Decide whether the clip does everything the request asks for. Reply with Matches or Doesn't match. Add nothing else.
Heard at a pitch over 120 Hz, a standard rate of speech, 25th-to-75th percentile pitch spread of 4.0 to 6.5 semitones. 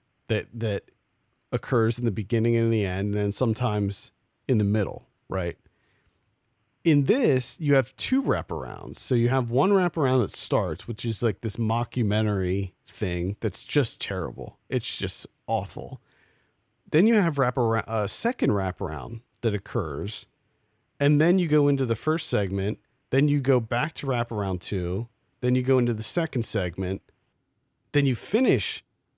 Doesn't match